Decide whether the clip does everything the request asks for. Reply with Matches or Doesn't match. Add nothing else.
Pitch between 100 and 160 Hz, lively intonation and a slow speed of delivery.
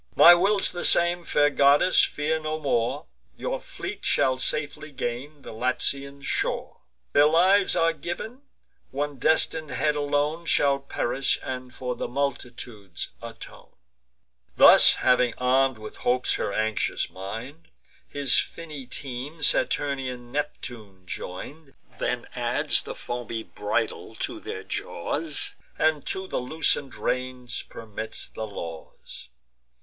Doesn't match